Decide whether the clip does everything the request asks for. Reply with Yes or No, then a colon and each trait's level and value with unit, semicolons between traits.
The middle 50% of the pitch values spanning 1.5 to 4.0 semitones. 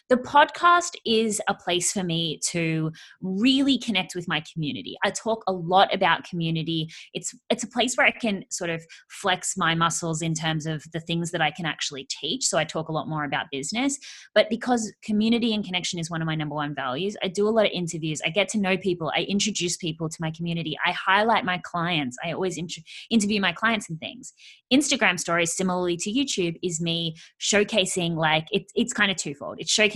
No: average, 4.8 semitones